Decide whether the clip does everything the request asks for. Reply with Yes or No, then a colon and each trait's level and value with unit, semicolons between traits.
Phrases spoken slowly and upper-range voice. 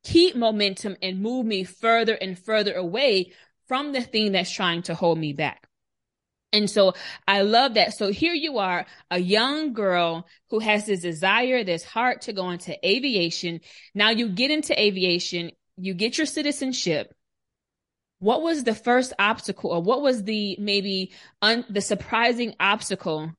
No: average, 160 wpm; high, 205 Hz